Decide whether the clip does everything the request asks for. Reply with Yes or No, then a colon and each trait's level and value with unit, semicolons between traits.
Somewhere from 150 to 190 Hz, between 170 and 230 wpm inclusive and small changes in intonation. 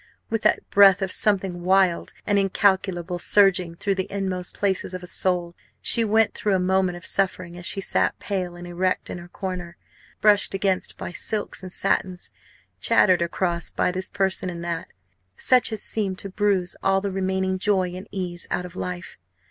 Yes: medium, 185 Hz; average, 180 wpm; narrow, 1.7 semitones